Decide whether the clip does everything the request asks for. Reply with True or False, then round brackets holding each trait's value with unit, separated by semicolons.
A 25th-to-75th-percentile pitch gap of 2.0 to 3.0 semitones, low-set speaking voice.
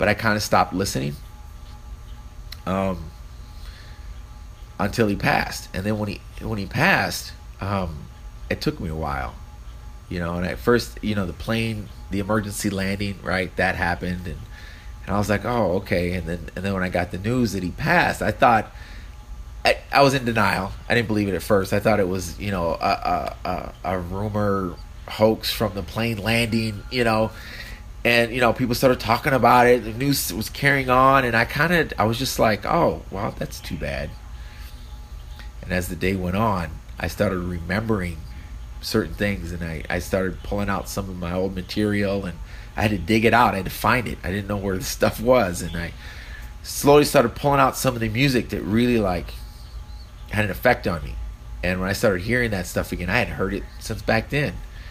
False (4.3 semitones; 100 Hz)